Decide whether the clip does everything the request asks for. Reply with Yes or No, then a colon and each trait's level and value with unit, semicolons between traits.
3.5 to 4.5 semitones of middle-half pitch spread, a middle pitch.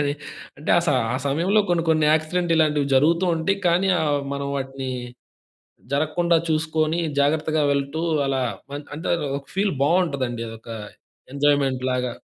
No: average, 3.1 semitones; medium, 150 Hz